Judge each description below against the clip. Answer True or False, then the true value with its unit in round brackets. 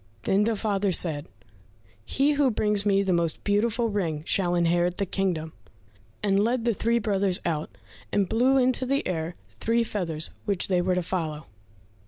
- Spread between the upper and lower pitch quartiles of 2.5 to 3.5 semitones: False (4.5 semitones)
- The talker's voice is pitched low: False (195 Hz)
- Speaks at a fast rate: False (170 wpm)